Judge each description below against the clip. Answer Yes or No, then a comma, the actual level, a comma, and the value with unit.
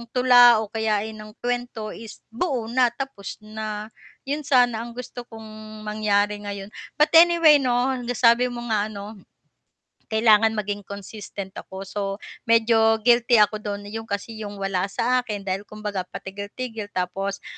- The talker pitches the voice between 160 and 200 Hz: No, high, 220 Hz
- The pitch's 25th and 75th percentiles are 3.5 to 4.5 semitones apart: No, average, 2.9 semitones